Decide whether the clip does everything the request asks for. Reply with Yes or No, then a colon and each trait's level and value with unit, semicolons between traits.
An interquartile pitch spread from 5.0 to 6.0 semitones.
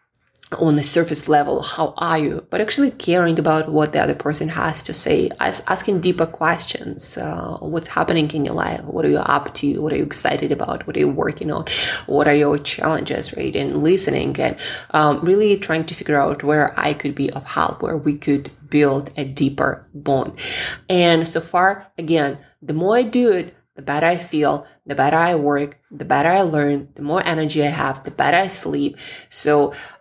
No: average, 2.7 semitones